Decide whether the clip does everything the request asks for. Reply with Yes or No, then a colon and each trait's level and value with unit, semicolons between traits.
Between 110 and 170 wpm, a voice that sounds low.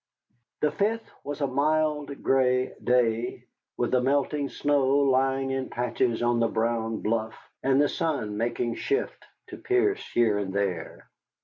Yes: average, 145 wpm; low, 130 Hz